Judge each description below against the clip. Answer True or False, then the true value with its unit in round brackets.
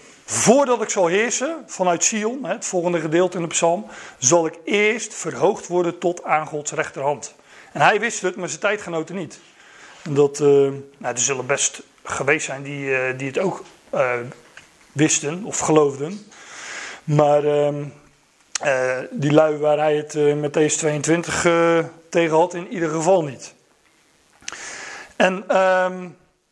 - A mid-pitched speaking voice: True (160 Hz)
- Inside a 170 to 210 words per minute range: False (155 wpm)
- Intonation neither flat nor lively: True (3.8 semitones)